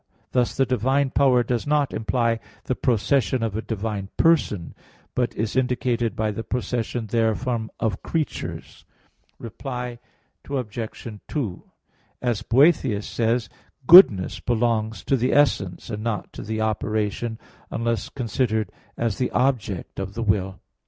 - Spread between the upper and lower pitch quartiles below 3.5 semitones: Yes, average, 2.8 semitones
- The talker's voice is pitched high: No, low, 115 Hz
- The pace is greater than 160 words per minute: No, average, 140 wpm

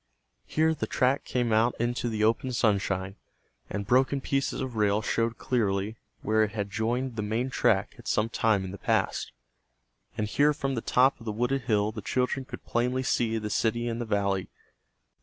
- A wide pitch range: No, average, 3.1 semitones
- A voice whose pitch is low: Yes, low, 115 Hz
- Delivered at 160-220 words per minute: Yes, average, 190 wpm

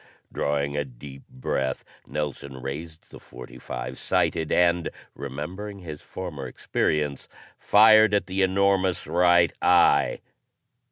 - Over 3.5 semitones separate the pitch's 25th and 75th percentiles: Yes, average, 5.1 semitones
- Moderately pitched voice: No, very low, 75 Hz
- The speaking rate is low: Yes, slow, 110 wpm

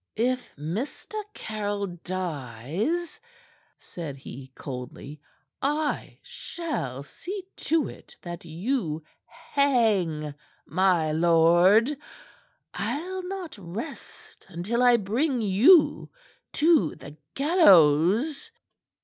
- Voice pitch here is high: Yes, high, 200 Hz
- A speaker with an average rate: No, slow, 85 wpm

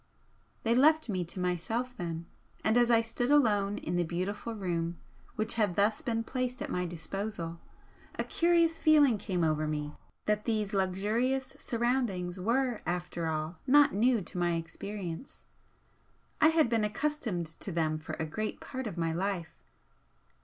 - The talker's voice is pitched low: No, high, 205 Hz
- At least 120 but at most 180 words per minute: Yes, average, 160 wpm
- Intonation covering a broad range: Yes, wide, 5.7 semitones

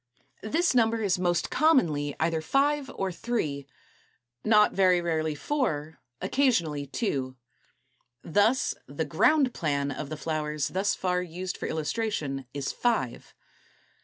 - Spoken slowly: Yes, slow, 125 wpm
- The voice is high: No, medium, 175 Hz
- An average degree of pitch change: No, wide, 7.1 semitones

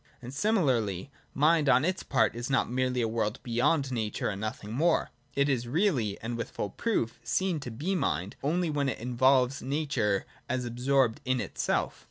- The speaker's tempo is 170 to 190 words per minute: Yes, average, 180 wpm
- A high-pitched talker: No, low, 130 Hz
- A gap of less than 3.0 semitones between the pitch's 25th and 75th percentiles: No, average, 4.0 semitones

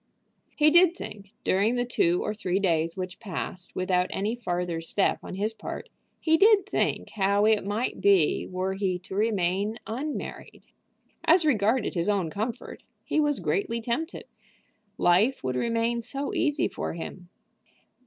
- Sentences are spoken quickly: No, average, 155 wpm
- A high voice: Yes, high, 205 Hz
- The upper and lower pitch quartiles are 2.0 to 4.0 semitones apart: No, average, 4.9 semitones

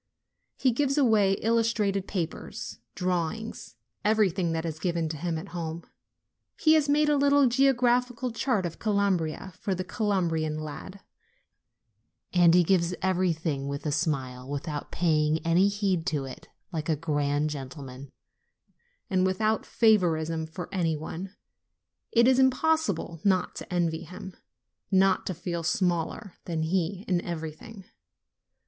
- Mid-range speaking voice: Yes, medium, 180 Hz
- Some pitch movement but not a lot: Yes, average, 4.6 semitones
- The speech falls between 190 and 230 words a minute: No, slow, 135 wpm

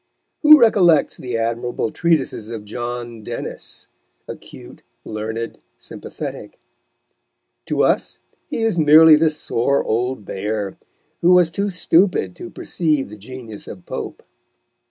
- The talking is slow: Yes, slow, 120 wpm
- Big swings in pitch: Yes, wide, 6.8 semitones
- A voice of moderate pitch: No, low, 125 Hz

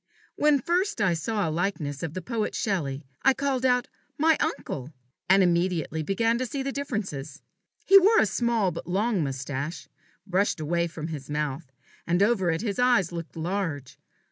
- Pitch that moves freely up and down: Yes, wide, 7.0 semitones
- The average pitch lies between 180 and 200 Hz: Yes, high, 190 Hz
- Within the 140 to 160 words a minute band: No, average, 170 wpm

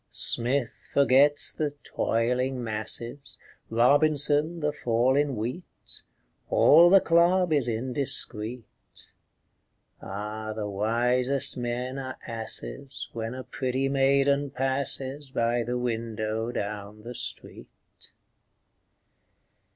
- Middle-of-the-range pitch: No, low, 125 Hz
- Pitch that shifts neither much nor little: Yes, average, 3.4 semitones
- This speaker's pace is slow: Yes, slow, 95 wpm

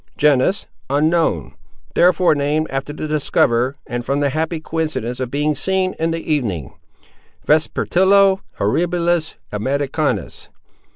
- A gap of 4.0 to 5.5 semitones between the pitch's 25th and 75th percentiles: No, average, 3.6 semitones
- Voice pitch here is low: No, medium, 150 Hz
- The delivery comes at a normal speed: No, slow, 105 wpm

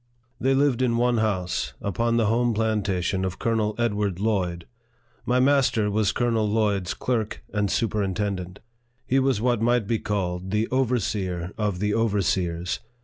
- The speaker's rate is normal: Yes, average, 150 wpm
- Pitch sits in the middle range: No, low, 105 Hz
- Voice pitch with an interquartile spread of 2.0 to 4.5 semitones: Yes, average, 3.4 semitones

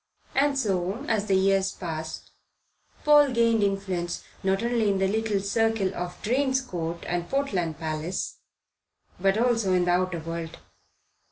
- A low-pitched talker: No, high, 195 Hz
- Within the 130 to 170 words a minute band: Yes, average, 145 wpm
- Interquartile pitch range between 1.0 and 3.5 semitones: No, average, 4.4 semitones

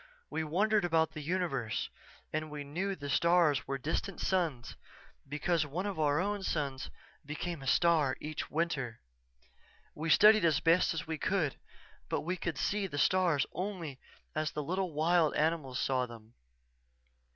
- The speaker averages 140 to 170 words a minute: Yes, average, 150 wpm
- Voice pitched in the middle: Yes, medium, 160 Hz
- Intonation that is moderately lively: Yes, average, 3.7 semitones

